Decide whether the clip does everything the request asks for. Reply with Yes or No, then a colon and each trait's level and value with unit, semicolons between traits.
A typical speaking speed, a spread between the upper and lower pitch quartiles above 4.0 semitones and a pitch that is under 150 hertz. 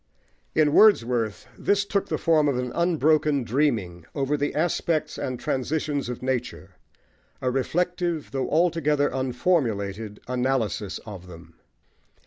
No: slow, 120 wpm; average, 5.0 semitones; low, 135 Hz